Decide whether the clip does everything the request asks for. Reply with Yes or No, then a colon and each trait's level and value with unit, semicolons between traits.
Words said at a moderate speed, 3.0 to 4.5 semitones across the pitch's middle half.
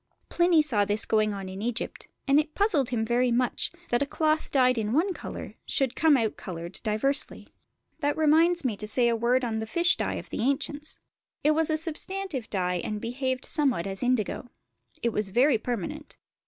No: average, 195 wpm; wide, 5.5 semitones